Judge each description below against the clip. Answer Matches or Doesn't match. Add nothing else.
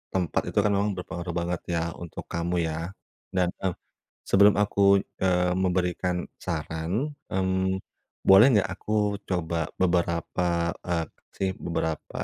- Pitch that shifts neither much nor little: Doesn't match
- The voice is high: Doesn't match